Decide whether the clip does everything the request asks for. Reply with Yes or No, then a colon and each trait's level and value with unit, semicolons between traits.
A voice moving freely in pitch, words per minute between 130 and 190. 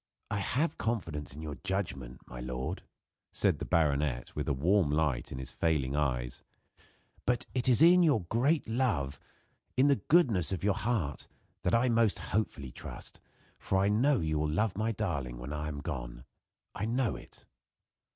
Yes: wide, 8.3 semitones; average, 170 wpm